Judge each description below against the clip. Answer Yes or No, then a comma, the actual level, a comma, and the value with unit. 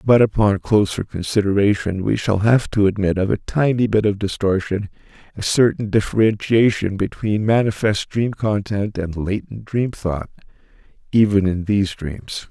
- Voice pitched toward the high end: No, low, 105 Hz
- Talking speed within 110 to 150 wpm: Yes, average, 145 wpm